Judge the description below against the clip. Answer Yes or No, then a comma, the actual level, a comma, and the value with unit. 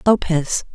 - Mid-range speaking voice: Yes, medium, 175 Hz